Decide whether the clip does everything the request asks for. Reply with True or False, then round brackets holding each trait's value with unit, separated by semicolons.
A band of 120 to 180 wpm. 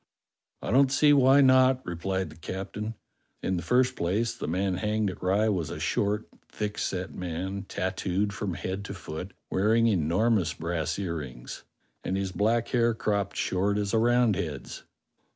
True (160 wpm)